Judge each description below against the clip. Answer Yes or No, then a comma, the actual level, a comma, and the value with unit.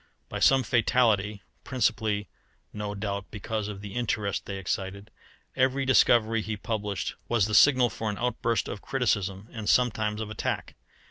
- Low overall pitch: Yes, low, 110 Hz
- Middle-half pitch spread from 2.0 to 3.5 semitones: Yes, average, 2.7 semitones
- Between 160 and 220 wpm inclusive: No, average, 150 wpm